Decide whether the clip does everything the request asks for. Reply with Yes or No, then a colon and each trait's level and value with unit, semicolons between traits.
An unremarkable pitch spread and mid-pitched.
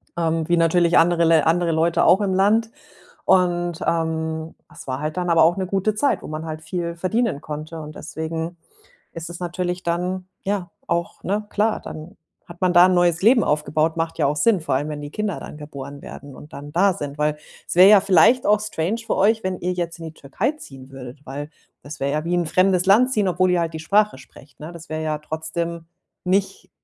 Yes: average, 3.0 semitones; medium, 170 Hz